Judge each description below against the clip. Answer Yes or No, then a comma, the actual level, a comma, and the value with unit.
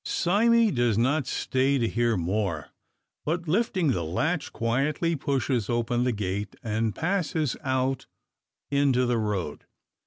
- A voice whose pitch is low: Yes, low, 125 Hz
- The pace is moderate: No, slow, 130 wpm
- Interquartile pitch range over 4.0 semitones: Yes, wide, 5.5 semitones